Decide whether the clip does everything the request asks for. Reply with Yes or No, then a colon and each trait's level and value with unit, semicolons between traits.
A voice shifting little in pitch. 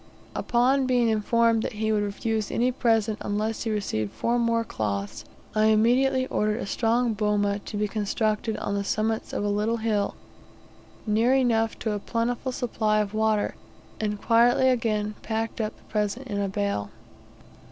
Yes: narrow, 2.0 semitones